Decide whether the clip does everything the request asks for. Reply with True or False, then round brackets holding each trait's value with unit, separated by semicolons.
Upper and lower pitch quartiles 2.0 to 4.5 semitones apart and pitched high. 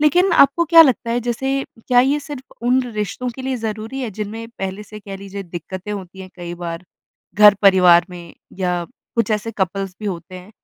False (5.2 semitones; 210 Hz)